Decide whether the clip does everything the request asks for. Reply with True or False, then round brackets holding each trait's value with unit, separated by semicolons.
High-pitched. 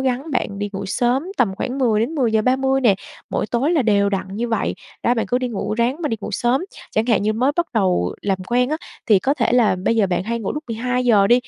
True (235 Hz)